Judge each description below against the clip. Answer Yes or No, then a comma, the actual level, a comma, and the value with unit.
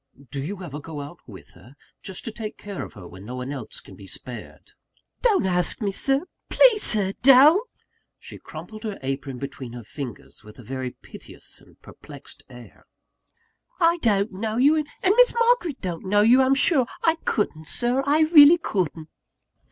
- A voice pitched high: Yes, high, 205 Hz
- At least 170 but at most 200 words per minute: Yes, average, 175 wpm